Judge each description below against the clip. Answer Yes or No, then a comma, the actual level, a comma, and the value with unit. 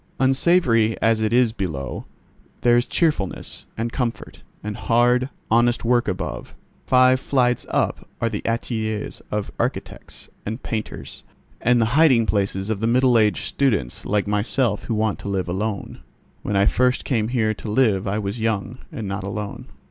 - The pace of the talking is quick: No, average, 160 wpm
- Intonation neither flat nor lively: Yes, average, 3.0 semitones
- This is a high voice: No, low, 110 Hz